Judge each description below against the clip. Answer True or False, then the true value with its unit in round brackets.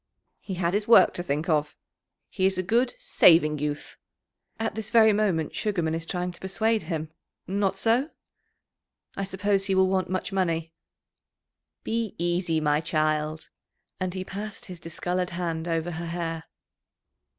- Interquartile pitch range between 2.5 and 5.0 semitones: True (3.3 semitones)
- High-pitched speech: False (180 Hz)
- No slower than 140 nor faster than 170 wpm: True (155 wpm)